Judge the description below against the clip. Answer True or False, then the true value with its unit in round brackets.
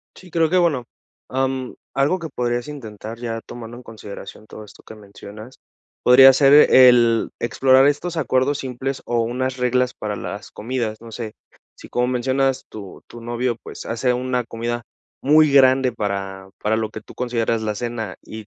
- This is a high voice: False (120 Hz)